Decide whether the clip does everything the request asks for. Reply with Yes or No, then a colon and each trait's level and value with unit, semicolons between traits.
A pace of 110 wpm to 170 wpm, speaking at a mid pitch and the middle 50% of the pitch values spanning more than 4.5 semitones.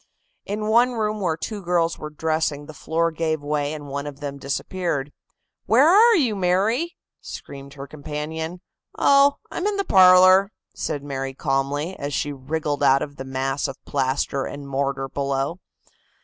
Yes: average, 165 wpm; medium, 155 Hz; average, 5.2 semitones